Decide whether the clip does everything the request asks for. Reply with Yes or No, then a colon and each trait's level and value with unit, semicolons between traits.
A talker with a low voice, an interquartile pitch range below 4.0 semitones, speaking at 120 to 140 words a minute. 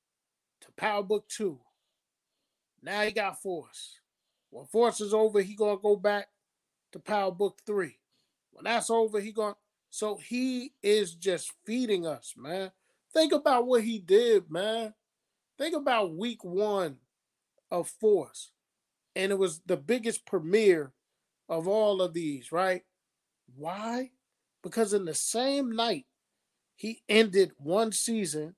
No: high, 205 Hz; average, 3.4 semitones; slow, 135 wpm